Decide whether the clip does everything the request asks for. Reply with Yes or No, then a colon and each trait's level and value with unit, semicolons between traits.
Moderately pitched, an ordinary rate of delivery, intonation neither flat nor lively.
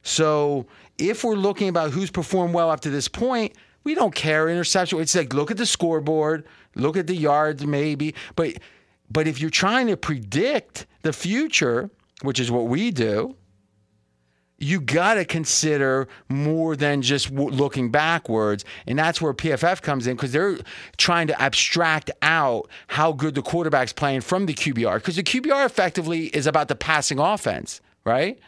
Yes: medium, 155 Hz; average, 170 wpm; average, 4.0 semitones